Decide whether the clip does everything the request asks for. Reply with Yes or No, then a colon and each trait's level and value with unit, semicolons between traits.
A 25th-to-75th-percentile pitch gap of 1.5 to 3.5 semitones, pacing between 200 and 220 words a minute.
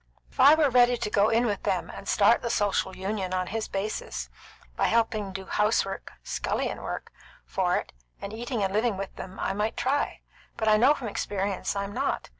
Yes: average, 3.2 semitones; fast, 205 wpm